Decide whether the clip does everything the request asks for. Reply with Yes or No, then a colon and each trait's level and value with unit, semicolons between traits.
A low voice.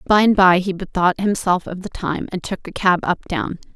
No: medium, 185 Hz